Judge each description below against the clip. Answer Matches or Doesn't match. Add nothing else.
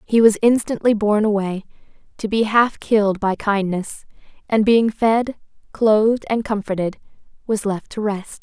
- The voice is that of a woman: Matches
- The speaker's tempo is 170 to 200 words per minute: Doesn't match